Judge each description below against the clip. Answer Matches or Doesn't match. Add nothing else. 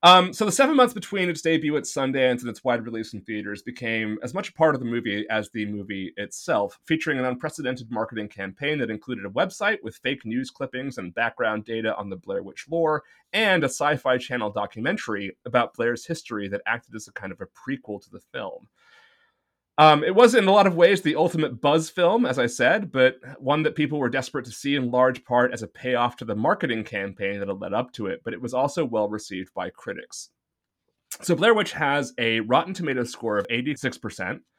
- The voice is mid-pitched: Doesn't match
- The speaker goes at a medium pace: Doesn't match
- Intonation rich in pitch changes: Matches